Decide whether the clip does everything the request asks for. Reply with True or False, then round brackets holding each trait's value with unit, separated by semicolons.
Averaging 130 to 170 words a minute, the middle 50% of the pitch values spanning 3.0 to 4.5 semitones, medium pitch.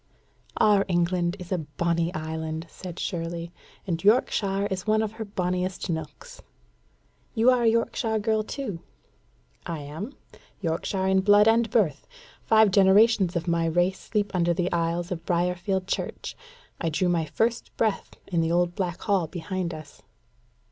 True (155 wpm; 3.5 semitones; 180 Hz)